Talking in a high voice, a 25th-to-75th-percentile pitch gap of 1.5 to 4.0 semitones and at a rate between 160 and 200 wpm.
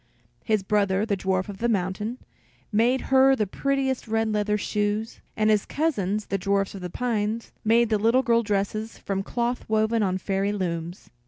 Yes: high, 215 Hz; average, 2.8 semitones; average, 175 wpm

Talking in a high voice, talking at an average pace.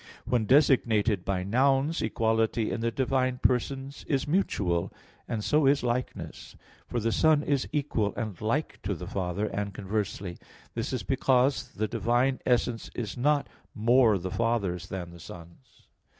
No: low, 115 Hz; average, 150 wpm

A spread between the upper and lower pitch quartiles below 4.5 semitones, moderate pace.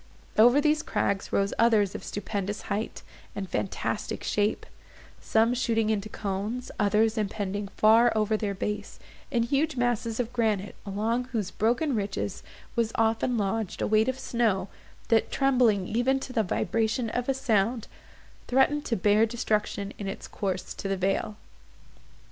Yes: average, 2.9 semitones; average, 150 wpm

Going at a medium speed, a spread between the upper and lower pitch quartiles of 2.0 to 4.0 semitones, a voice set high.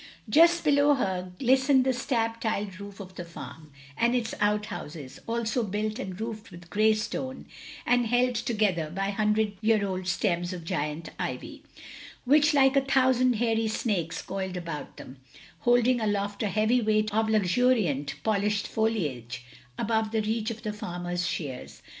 No: average, 155 wpm; average, 4.4 semitones; high, 215 Hz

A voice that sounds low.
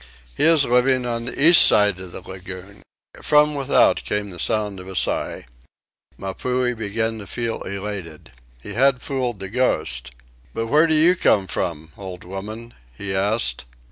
Yes: low, 105 Hz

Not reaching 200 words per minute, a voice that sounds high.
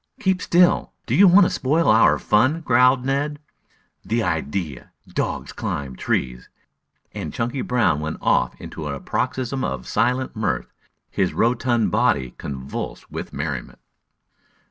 No: slow, 135 wpm; low, 115 Hz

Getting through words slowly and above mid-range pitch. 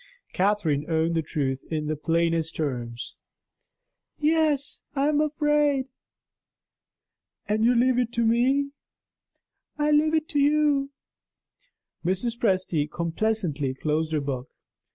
Yes: slow, 115 wpm; high, 210 Hz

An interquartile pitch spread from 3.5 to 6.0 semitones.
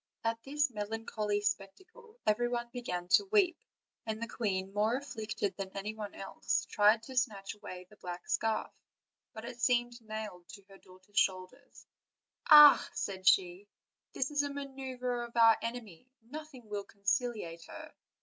Yes: average, 3.8 semitones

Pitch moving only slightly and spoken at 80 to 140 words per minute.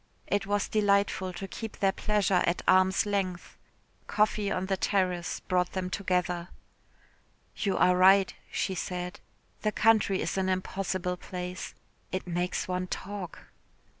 Yes: narrow, 1.7 semitones; slow, 135 wpm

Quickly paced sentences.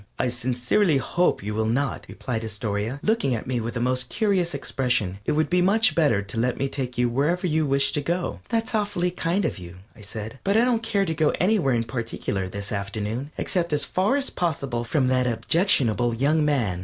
Yes: fast, 210 wpm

